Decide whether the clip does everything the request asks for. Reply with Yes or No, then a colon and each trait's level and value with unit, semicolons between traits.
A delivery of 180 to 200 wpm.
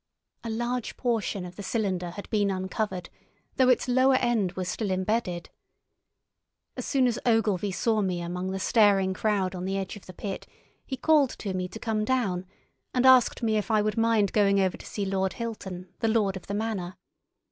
Yes: average, 195 wpm